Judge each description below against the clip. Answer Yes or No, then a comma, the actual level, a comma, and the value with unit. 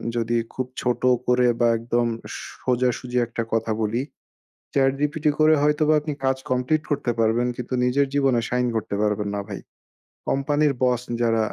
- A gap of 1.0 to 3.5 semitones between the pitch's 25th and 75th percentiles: Yes, average, 3.2 semitones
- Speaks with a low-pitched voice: Yes, low, 125 Hz